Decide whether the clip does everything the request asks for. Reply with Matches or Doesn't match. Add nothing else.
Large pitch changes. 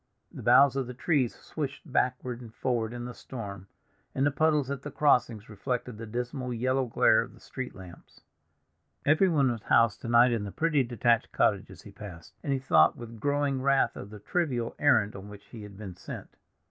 Doesn't match